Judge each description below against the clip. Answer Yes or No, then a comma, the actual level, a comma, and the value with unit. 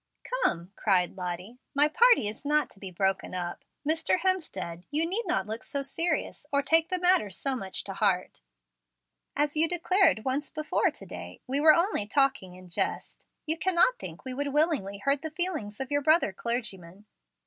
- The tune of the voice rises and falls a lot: Yes, wide, 8.7 semitones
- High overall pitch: Yes, very high, 275 Hz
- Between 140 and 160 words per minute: No, average, 180 wpm